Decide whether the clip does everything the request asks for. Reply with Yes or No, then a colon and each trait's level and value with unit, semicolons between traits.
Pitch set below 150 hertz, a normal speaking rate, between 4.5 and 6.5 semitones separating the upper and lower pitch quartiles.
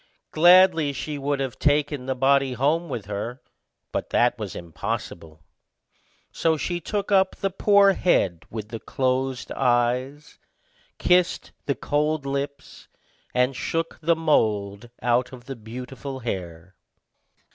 No: low, 135 Hz; slow, 130 wpm; average, 4.8 semitones